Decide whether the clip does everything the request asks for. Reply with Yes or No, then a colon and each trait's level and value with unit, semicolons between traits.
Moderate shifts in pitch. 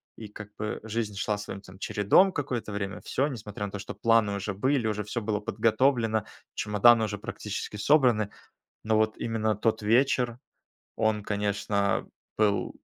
No: narrow, 2.0 semitones